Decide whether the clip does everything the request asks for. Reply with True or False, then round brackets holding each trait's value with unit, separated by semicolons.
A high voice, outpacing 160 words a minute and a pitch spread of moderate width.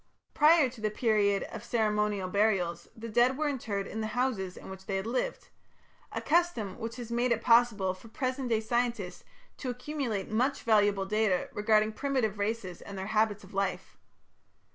True (220 Hz; 175 wpm; 3.3 semitones)